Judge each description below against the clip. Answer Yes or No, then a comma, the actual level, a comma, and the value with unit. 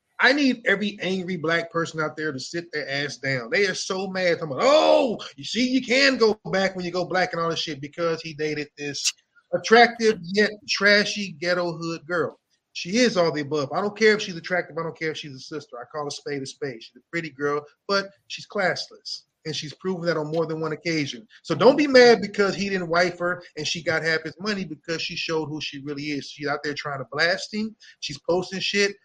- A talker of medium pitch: Yes, medium, 170 Hz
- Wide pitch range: No, average, 4.6 semitones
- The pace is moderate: No, fast, 240 wpm